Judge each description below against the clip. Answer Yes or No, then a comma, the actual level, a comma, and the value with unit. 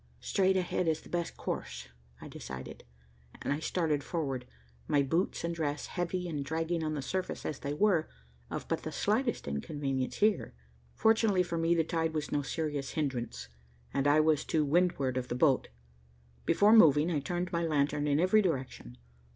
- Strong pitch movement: No, average, 3.8 semitones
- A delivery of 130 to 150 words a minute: No, average, 175 wpm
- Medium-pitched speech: Yes, medium, 155 Hz